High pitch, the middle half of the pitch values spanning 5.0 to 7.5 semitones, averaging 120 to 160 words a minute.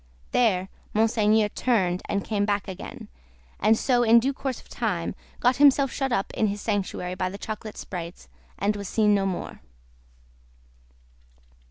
No: high, 210 Hz; average, 3.2 semitones; average, 155 wpm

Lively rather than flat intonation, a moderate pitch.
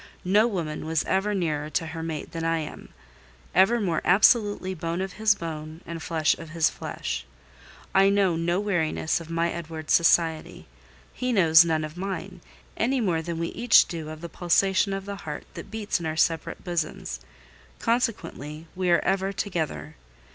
No: average, 3.3 semitones; medium, 170 Hz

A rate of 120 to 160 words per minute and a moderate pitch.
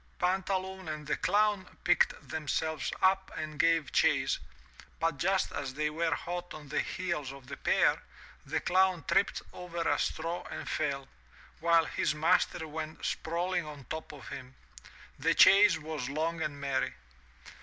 Yes: average, 155 wpm; medium, 160 Hz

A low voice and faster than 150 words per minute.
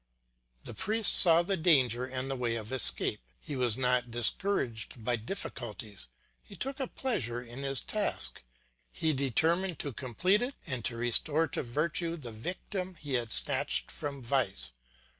Yes: low, 130 Hz; average, 160 wpm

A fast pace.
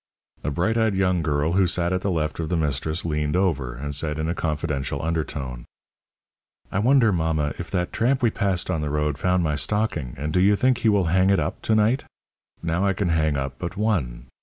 Yes: fast, 220 wpm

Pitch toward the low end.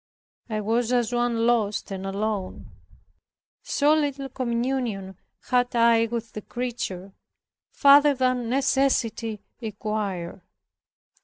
No: high, 235 Hz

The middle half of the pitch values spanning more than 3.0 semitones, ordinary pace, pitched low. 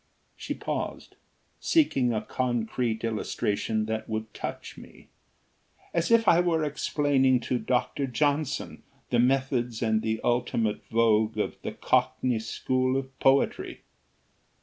No: average, 3.4 semitones; slow, 125 wpm; low, 125 Hz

